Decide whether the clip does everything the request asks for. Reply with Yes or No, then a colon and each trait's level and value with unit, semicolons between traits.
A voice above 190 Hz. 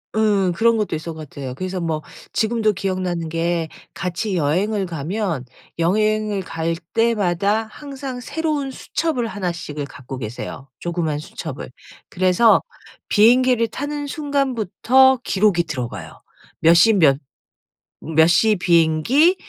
No: medium, 185 Hz